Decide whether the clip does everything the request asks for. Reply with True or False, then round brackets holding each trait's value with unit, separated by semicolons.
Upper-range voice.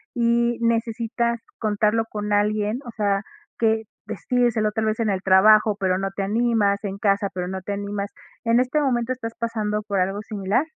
True (215 Hz)